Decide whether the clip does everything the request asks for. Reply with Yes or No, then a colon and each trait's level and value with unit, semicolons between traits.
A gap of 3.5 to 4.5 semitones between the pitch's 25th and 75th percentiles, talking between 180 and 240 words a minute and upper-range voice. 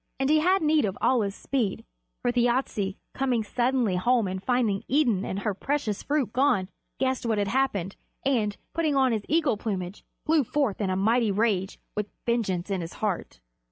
No: average, 5.1 semitones; average, 185 wpm; high, 230 Hz